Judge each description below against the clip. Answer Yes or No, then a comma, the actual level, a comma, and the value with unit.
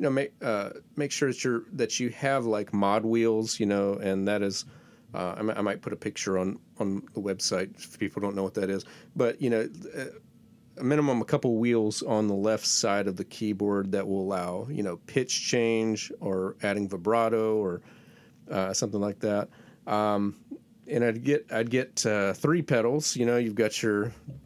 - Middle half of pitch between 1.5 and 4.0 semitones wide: Yes, average, 3.1 semitones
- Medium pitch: No, low, 110 Hz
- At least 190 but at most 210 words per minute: Yes, average, 200 wpm